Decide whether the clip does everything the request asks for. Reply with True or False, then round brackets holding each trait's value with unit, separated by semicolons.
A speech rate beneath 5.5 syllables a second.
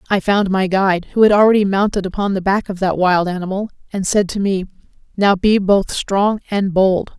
True (5.3 syllables/s)